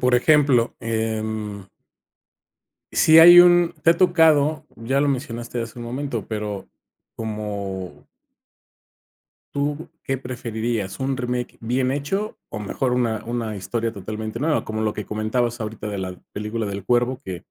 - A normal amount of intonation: Yes, average, 4.0 semitones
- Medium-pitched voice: No, low, 115 Hz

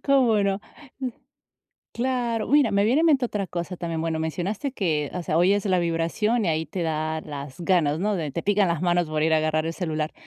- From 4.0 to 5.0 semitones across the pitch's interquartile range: Yes, average, 4.7 semitones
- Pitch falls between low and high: Yes, medium, 175 Hz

